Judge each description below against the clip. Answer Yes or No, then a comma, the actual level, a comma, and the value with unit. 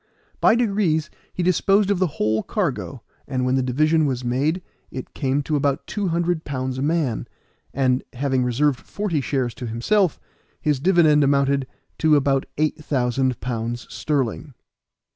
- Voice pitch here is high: No, medium, 140 Hz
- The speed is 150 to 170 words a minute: Yes, average, 155 wpm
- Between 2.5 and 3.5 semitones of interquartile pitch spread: No, average, 4.0 semitones